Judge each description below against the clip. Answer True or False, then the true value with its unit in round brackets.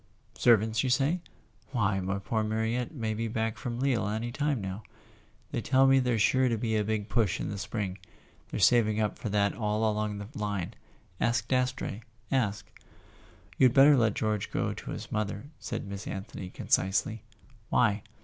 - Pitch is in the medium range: False (110 Hz)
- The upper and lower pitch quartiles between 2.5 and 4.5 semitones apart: True (2.8 semitones)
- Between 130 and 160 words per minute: False (180 wpm)